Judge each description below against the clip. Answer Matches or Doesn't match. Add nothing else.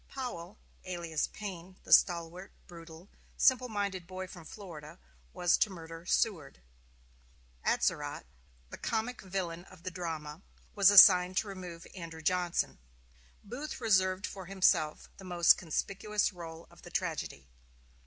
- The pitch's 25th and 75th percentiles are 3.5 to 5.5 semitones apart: Doesn't match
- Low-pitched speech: Doesn't match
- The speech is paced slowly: Matches